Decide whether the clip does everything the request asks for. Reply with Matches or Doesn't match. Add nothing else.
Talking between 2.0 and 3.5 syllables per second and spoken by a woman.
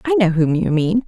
Doesn't match